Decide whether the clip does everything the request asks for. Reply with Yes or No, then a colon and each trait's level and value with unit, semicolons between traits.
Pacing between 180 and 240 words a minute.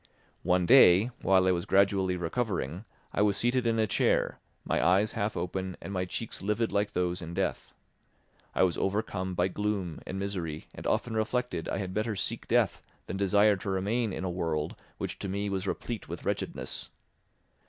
Yes: average, 185 wpm